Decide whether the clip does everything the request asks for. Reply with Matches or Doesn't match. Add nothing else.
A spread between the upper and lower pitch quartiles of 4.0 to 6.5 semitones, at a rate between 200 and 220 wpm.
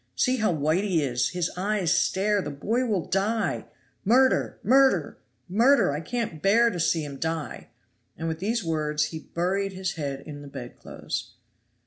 Doesn't match